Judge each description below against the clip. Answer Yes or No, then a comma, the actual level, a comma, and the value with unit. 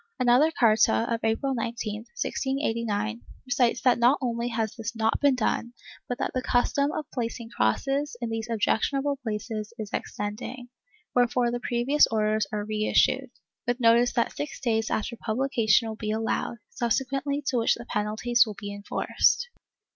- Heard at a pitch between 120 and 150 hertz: No, high, 235 Hz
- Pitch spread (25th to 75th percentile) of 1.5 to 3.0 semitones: Yes, narrow, 2.6 semitones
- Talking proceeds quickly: No, average, 160 wpm